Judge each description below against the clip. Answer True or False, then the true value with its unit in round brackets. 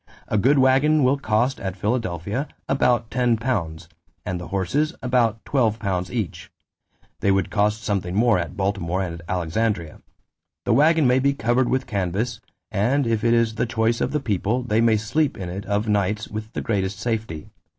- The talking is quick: False (175 wpm)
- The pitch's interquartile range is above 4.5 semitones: False (4.2 semitones)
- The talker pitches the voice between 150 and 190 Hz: False (110 Hz)